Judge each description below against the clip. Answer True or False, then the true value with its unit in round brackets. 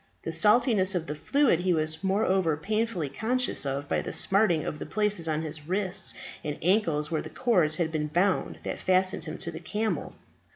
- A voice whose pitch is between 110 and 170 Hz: False (180 Hz)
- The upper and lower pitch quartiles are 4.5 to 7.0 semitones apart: True (5.0 semitones)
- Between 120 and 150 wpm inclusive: False (195 wpm)